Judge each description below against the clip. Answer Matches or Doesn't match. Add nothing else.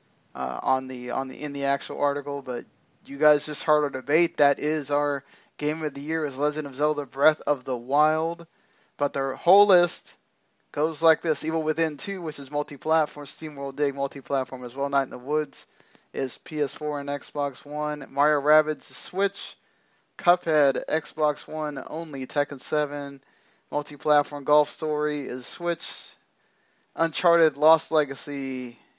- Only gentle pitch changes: Matches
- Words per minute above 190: Doesn't match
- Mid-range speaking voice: Matches